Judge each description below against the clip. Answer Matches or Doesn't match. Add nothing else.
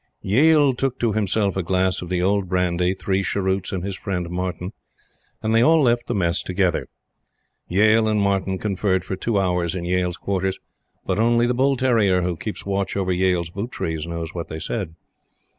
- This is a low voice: Matches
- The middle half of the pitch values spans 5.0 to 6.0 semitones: Doesn't match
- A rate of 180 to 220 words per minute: Matches